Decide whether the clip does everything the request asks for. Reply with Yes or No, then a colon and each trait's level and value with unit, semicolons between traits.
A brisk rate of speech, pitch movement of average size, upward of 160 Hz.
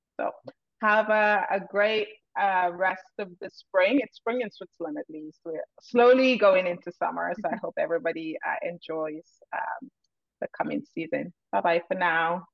No: average, 170 wpm; average, 4.0 semitones; high, 190 Hz